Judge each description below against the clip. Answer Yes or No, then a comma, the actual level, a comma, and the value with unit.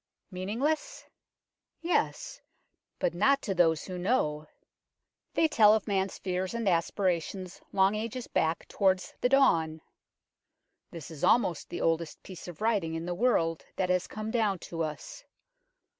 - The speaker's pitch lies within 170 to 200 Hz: Yes, high, 190 Hz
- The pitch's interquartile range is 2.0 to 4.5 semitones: No, average, 5.0 semitones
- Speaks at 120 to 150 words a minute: Yes, average, 145 wpm